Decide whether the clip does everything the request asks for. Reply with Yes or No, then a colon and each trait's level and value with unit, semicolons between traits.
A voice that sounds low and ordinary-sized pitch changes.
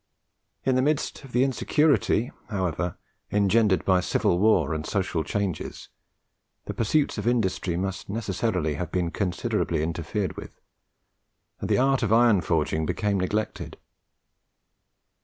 Yes: low, 100 Hz; average, 4.9 semitones